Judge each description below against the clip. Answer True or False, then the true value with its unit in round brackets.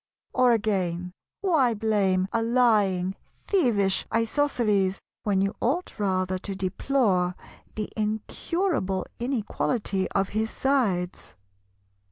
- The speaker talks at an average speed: False (100 wpm)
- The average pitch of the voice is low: False (210 Hz)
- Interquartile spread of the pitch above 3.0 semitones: True (4.3 semitones)